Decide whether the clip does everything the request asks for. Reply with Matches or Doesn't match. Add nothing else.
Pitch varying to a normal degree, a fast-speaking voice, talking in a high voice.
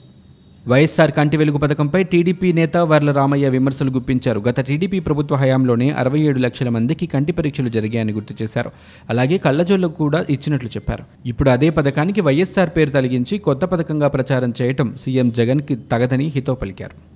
Doesn't match